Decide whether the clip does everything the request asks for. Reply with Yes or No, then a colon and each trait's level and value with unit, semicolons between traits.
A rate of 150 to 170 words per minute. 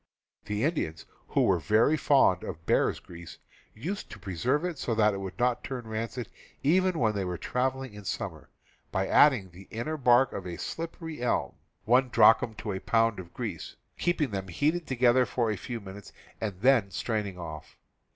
No: average, 180 wpm